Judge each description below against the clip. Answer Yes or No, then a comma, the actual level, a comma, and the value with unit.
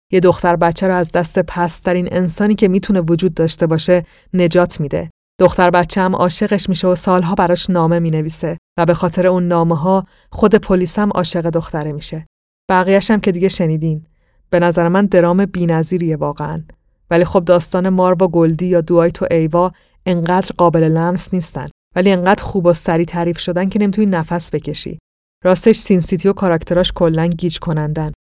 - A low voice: No, medium, 175 Hz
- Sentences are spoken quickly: Yes, fast, 170 wpm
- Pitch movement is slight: Yes, narrow, 1.8 semitones